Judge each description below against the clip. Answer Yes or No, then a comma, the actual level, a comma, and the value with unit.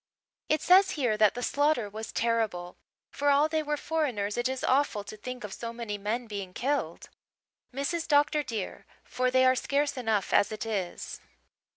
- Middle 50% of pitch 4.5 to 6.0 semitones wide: Yes, average, 5.2 semitones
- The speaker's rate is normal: Yes, average, 180 wpm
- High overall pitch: Yes, high, 245 Hz